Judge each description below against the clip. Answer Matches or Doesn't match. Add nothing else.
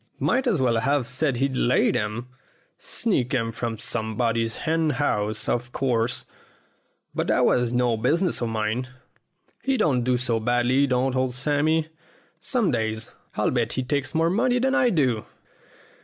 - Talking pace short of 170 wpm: Matches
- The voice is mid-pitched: Doesn't match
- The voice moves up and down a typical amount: Matches